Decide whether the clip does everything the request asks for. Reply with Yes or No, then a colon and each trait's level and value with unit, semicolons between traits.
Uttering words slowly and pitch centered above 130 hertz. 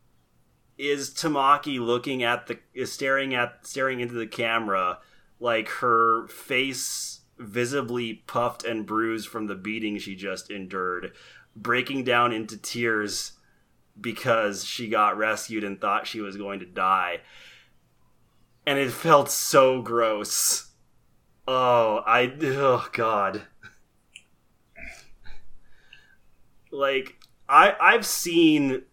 No: slow, 110 wpm; low, 120 Hz